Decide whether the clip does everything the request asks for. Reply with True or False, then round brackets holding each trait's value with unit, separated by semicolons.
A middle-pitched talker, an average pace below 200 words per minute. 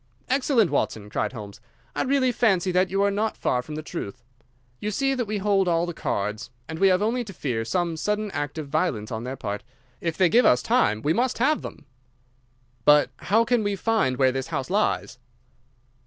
False (175 Hz; 205 wpm)